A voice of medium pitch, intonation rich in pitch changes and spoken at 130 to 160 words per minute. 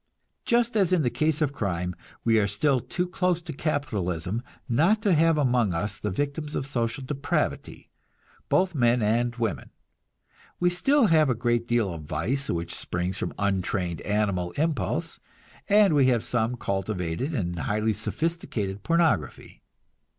No: low, 120 Hz; wide, 7.6 semitones; average, 150 wpm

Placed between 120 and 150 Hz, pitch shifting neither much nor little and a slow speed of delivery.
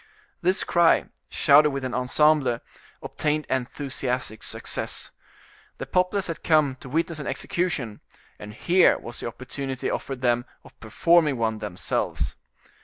Yes: low, 135 Hz; average, 4.4 semitones; slow, 130 wpm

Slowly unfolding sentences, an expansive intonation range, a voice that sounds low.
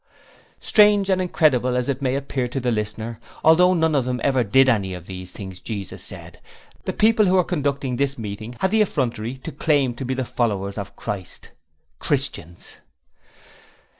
No: average, 170 wpm; wide, 5.7 semitones; low, 130 Hz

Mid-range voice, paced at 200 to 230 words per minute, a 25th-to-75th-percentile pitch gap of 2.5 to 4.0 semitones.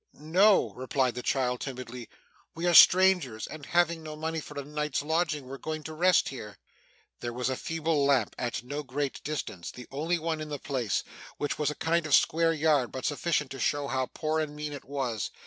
Yes: medium, 145 Hz; fast, 205 wpm; average, 3.5 semitones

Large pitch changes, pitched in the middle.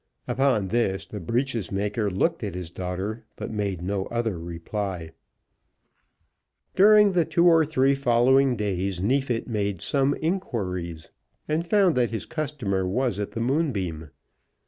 No: wide, 6.4 semitones; low, 115 Hz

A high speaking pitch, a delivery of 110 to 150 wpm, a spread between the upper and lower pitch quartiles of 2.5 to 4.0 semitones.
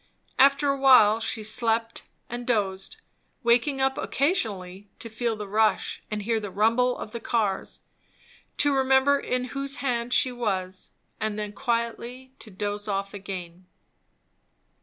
Yes: high, 230 Hz; average, 140 wpm; average, 3.6 semitones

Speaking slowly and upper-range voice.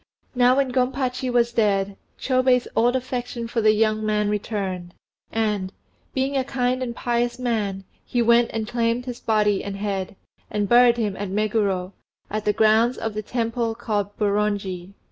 No: average, 165 wpm; high, 225 Hz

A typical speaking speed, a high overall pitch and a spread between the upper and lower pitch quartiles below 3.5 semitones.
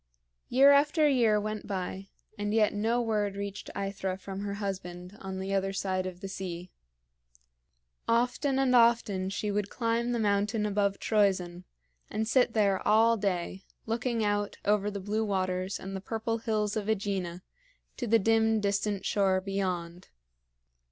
Yes: average, 155 wpm; high, 205 Hz; narrow, 2.6 semitones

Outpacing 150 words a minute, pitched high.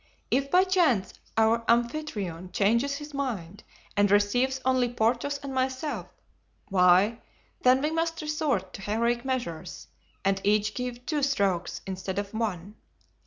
No: slow, 135 wpm; high, 235 Hz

